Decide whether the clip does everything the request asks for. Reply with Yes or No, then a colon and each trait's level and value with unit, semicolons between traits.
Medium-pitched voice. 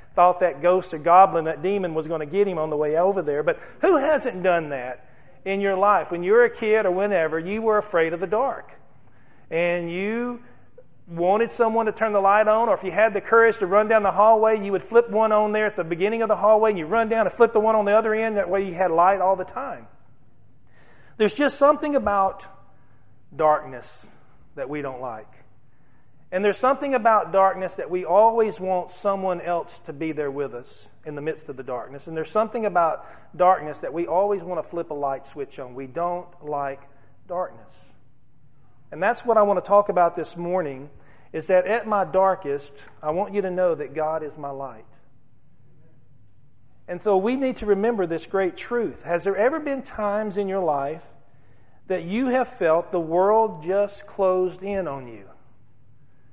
Yes: medium, 180 Hz